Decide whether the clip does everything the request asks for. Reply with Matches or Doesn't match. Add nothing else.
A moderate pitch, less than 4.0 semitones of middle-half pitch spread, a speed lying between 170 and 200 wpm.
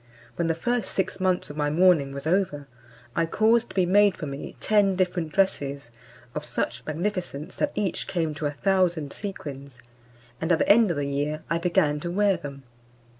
Doesn't match